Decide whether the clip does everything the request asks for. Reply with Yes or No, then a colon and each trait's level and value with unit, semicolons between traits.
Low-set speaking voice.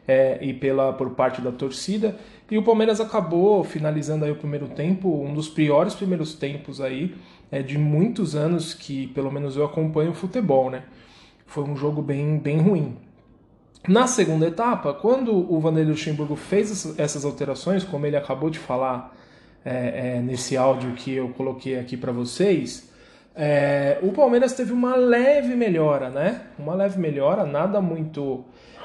No: medium, 150 Hz